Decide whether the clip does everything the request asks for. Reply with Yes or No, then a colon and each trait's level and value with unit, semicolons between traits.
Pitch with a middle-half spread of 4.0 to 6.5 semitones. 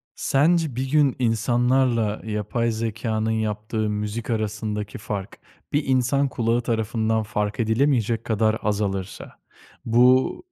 No: narrow, 2.5 semitones